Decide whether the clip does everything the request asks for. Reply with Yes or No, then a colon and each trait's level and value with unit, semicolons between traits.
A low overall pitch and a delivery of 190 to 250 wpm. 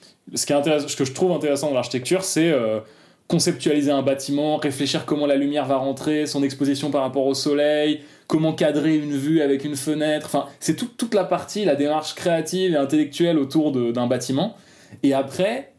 No: medium, 150 Hz; average, 195 wpm